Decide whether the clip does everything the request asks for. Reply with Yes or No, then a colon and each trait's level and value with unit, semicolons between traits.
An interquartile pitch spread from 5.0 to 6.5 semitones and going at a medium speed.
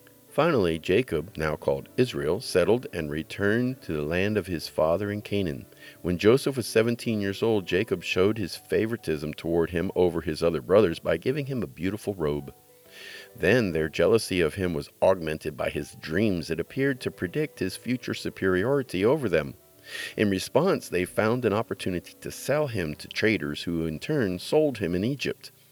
Yes: wide, 5.6 semitones; average, 175 wpm